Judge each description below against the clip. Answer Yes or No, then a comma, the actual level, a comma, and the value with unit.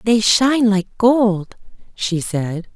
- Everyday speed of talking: No, slow, 130 wpm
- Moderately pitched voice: No, high, 210 Hz